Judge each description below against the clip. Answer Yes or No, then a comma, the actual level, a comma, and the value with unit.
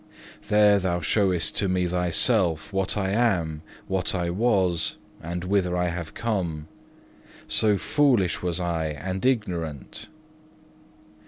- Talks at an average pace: No, slow, 120 wpm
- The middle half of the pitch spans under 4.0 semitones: Yes, average, 3.0 semitones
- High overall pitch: No, very low, 90 Hz